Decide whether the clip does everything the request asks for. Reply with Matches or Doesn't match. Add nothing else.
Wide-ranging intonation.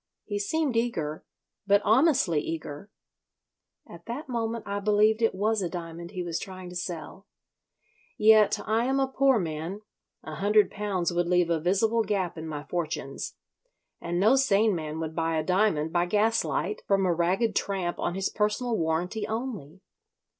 Doesn't match